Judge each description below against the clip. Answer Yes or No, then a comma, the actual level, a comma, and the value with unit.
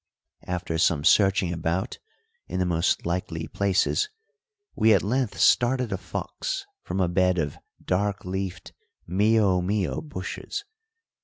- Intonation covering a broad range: No, average, 3.2 semitones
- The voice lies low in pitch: Yes, very low, 95 Hz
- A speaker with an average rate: No, slow, 130 wpm